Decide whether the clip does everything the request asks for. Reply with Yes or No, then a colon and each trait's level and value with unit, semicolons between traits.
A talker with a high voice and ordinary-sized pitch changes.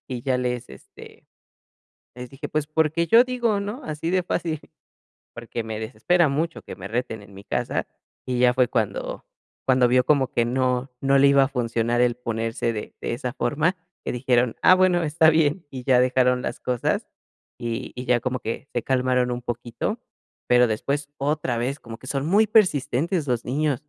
No: low, 130 Hz; average, 4.1 semitones